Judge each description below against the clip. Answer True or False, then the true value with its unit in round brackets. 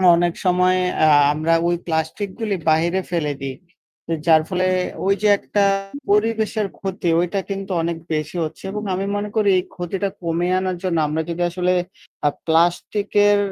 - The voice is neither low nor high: True (180 Hz)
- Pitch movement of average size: True (3.2 semitones)